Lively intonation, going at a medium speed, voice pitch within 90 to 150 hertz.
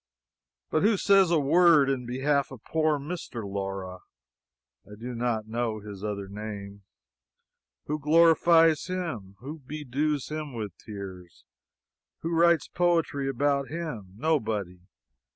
No: wide, 7.0 semitones; slow, 125 wpm; low, 135 Hz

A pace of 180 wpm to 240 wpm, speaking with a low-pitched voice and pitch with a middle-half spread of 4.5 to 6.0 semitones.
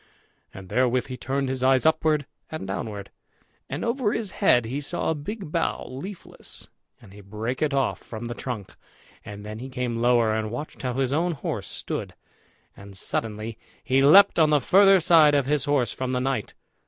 Yes: average, 190 wpm; low, 130 Hz; average, 4.9 semitones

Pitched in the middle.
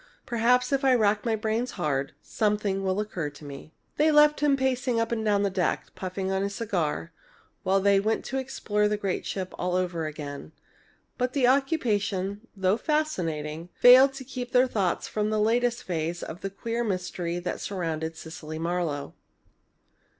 No: high, 205 Hz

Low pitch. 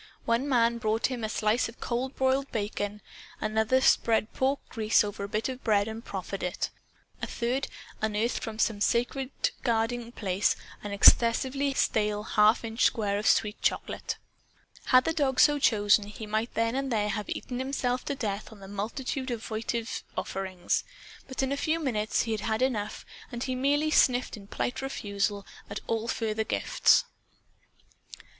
No: high, 225 Hz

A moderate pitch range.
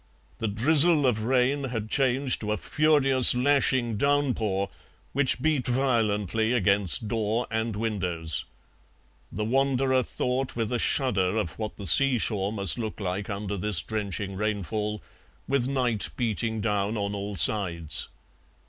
Yes: average, 4.1 semitones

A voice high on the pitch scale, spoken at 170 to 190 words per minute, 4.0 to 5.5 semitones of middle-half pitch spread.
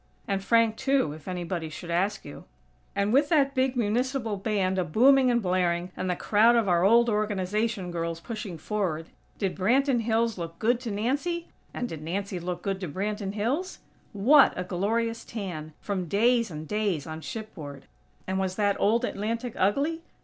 Yes: high, 205 Hz; average, 175 wpm; average, 4.5 semitones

